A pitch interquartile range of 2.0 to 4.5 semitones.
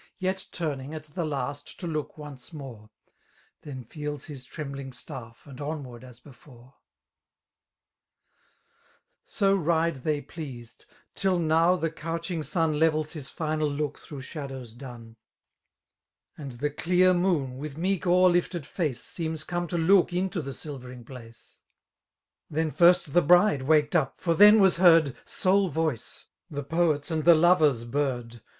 Yes: average, 4.0 semitones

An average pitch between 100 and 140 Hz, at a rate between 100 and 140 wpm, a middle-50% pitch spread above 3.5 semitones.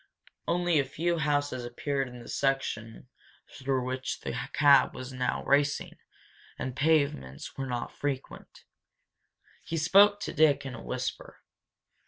No: low, 135 Hz; slow, 135 wpm; average, 2.7 semitones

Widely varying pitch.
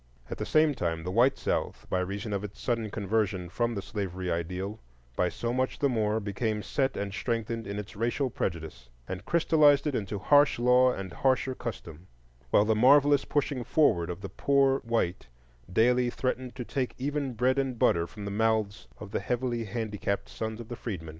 No: average, 4.3 semitones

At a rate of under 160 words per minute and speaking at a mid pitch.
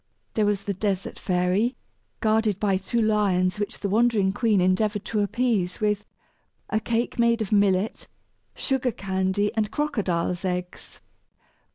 No: average, 140 wpm; high, 205 Hz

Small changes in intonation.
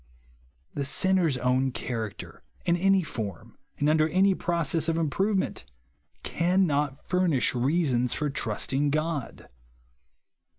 No: average, 4.7 semitones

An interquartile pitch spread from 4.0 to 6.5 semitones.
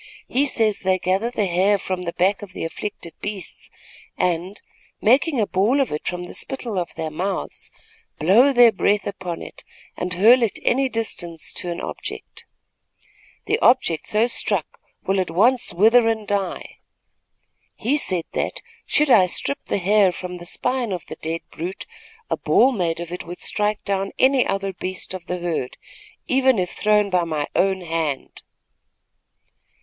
Yes: average, 4.3 semitones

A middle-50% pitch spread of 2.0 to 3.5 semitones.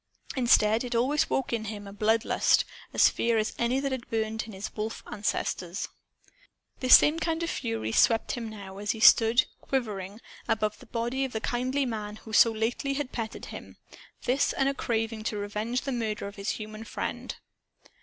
Yes: average, 2.8 semitones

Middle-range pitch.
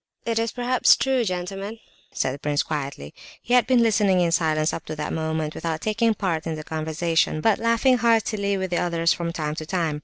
Yes: medium, 175 Hz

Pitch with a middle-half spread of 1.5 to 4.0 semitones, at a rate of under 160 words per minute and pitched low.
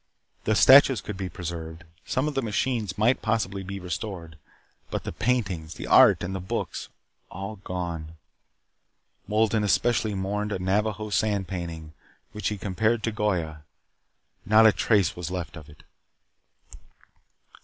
Yes: average, 3.6 semitones; average, 145 wpm; low, 100 Hz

